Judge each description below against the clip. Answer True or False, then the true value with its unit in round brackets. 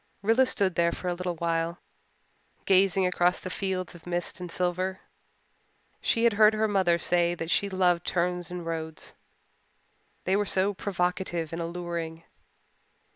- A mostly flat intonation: True (1.9 semitones)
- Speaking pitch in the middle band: True (180 Hz)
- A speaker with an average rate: True (150 wpm)